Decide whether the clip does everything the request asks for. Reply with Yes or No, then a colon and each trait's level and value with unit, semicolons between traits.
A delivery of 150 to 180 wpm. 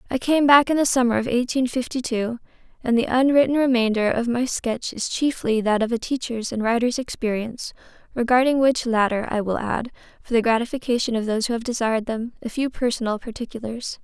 No: average, 190 wpm